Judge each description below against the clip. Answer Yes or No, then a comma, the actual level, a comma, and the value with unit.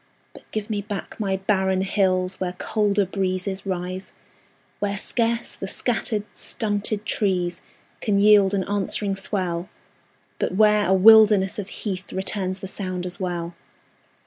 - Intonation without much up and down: Yes, narrow, 1.9 semitones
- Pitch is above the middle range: Yes, high, 195 Hz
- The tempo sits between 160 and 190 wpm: No, average, 140 wpm